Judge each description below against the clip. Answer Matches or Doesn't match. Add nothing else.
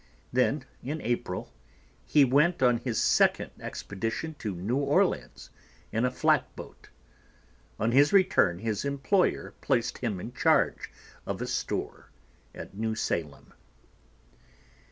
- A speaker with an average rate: Doesn't match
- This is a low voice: Matches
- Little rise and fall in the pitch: Doesn't match